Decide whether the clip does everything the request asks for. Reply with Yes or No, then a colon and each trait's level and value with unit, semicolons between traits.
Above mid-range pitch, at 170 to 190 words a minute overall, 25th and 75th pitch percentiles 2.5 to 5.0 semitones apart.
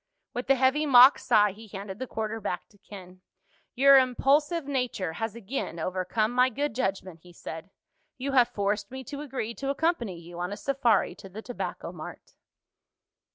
No: high, 230 Hz; average, 175 wpm; wide, 5.4 semitones